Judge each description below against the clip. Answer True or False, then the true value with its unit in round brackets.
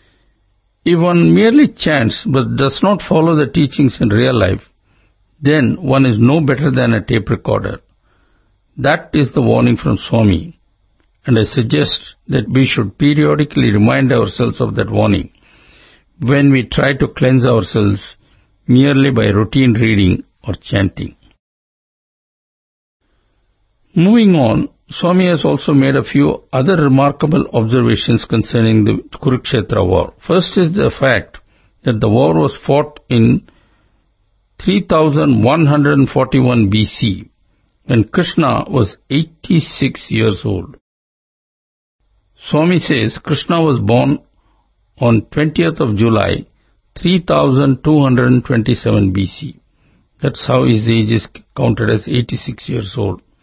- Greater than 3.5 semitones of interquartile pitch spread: True (5.5 semitones)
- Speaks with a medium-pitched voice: False (125 Hz)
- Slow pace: True (120 wpm)